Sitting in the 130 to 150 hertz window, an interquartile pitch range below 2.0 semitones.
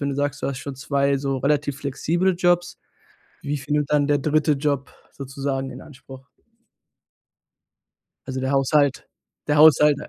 Yes: medium, 140 Hz; narrow, 1.6 semitones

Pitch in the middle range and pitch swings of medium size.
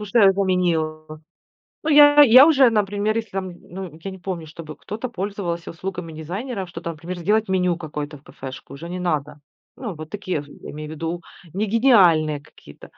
Yes: medium, 180 Hz; average, 4.7 semitones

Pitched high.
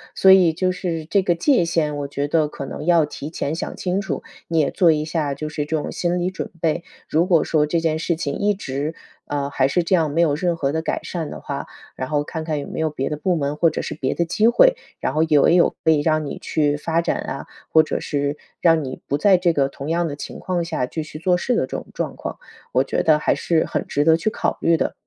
No: medium, 160 Hz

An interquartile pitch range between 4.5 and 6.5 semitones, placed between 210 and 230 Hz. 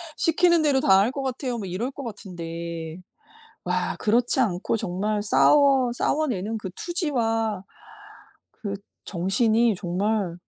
Yes: wide, 5.5 semitones; high, 220 Hz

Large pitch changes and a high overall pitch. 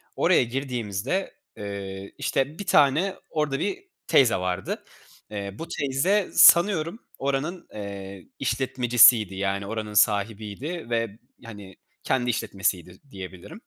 No: wide, 6.0 semitones; low, 115 Hz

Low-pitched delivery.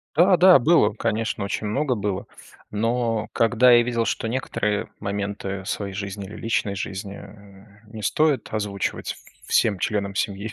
Yes: low, 105 Hz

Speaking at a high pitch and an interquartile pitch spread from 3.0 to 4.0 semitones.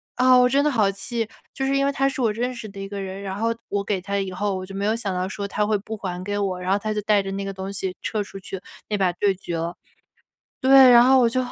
Yes: high, 205 Hz; average, 3.4 semitones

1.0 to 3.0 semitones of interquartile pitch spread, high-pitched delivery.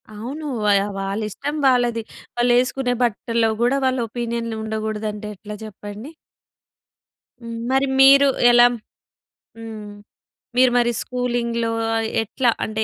Yes: narrow, 2.4 semitones; high, 235 Hz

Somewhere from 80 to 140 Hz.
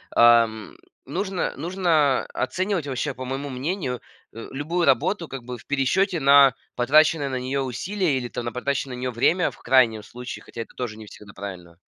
Yes: low, 135 Hz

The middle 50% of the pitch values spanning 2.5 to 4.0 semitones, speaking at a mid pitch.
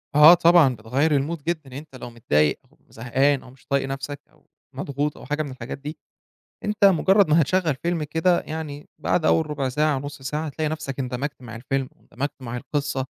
Yes: average, 3.1 semitones; medium, 145 Hz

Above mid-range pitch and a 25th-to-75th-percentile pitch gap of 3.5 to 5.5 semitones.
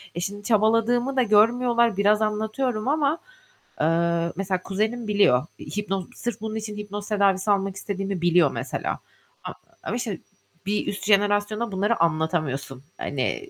No: high, 205 Hz; average, 2.8 semitones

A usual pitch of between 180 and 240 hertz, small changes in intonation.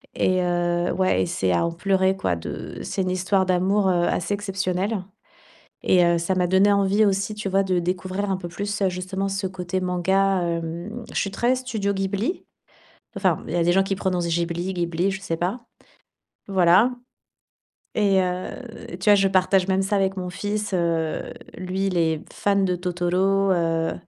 Yes: medium, 185 Hz; narrow, 1.9 semitones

